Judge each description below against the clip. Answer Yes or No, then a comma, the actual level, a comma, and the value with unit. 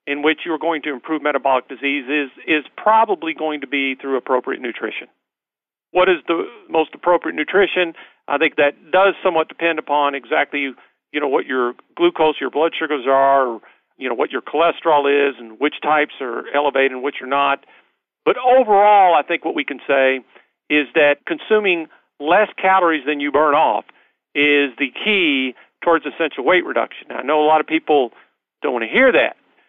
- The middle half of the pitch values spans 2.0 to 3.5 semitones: Yes, average, 3.1 semitones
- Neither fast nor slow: Yes, average, 185 wpm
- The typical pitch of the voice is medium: Yes, medium, 150 Hz